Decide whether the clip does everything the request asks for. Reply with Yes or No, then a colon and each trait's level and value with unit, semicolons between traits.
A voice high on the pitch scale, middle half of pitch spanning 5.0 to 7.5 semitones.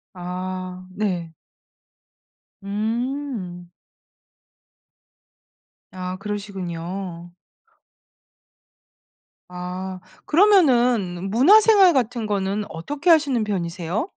Yes: high, 200 Hz; wide, 5.5 semitones